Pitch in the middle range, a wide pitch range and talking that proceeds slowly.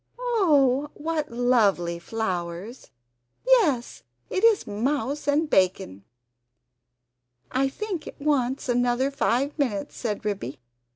No: very high, 255 Hz; wide, 6.1 semitones; slow, 105 wpm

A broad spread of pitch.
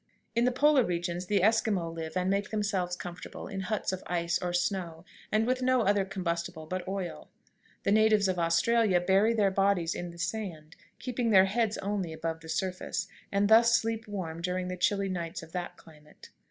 No: average, 3.7 semitones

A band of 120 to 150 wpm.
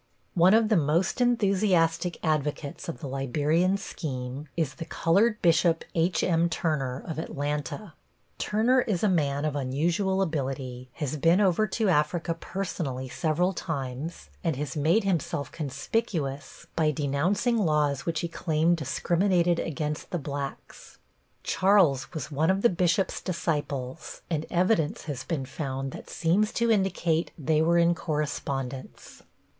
Yes: average, 140 wpm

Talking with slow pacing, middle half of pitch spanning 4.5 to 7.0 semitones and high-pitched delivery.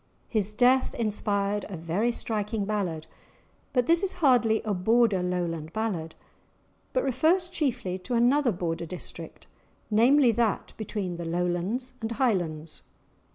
Yes: slow, 130 wpm; average, 5.3 semitones; high, 210 Hz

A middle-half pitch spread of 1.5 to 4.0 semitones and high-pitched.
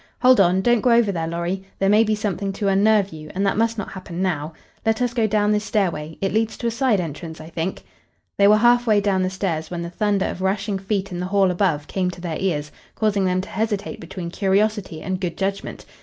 Yes: average, 3.1 semitones; high, 195 Hz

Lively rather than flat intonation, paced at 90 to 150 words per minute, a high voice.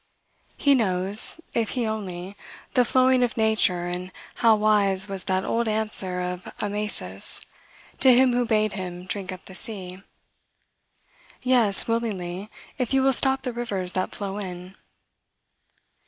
No: average, 4.0 semitones; average, 140 wpm; high, 210 Hz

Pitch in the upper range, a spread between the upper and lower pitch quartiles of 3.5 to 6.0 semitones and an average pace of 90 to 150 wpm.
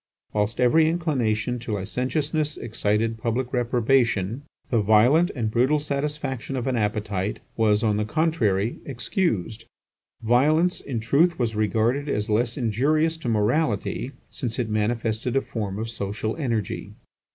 No: low, 120 Hz; average, 4.4 semitones; slow, 135 wpm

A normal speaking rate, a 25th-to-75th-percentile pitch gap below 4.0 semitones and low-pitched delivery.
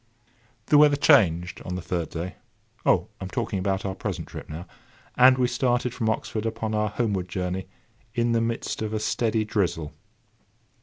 No: average, 165 wpm; average, 4.3 semitones; low, 110 Hz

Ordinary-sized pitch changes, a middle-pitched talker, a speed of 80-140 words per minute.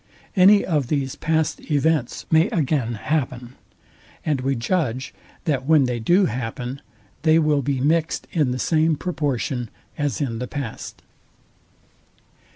Yes: average, 4.0 semitones; medium, 145 Hz; slow, 135 wpm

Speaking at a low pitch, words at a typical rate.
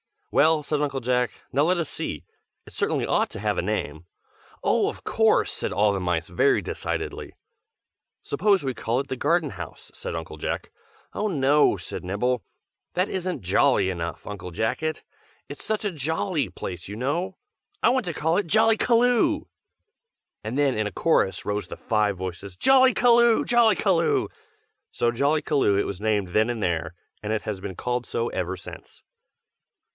Yes: low, 130 Hz; average, 170 wpm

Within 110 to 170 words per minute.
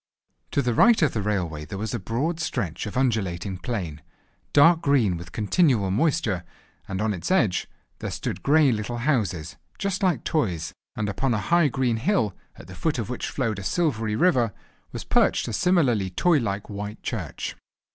No: average, 185 wpm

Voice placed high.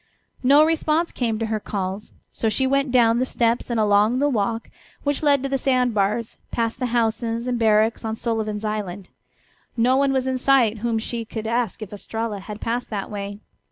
Yes: high, 230 Hz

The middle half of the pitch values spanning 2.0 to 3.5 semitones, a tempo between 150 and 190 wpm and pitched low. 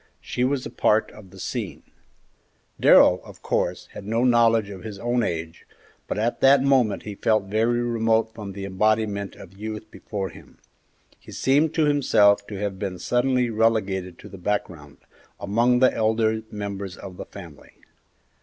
Yes: average, 3.1 semitones; average, 165 wpm; low, 110 Hz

